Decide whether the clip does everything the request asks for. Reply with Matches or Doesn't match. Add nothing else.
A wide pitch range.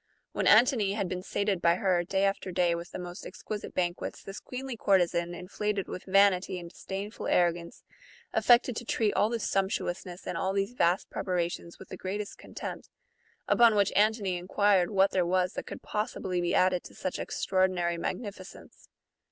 Doesn't match